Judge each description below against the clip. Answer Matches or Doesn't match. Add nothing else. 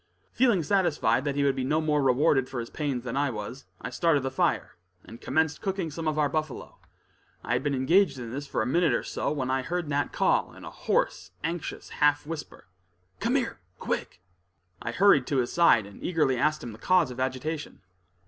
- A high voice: Doesn't match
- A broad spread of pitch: Doesn't match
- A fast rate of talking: Matches